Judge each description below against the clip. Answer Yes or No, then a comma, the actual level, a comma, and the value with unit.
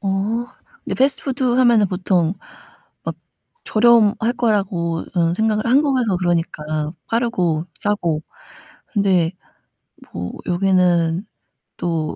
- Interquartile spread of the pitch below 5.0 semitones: No, average, 5.3 semitones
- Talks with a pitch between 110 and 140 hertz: No, high, 190 Hz